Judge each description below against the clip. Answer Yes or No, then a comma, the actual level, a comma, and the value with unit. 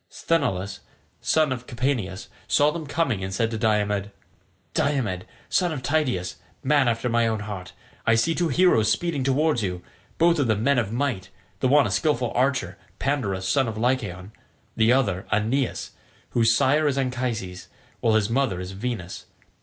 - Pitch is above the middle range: No, low, 120 Hz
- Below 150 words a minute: No, average, 165 wpm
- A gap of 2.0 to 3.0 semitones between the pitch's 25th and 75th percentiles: No, average, 5.3 semitones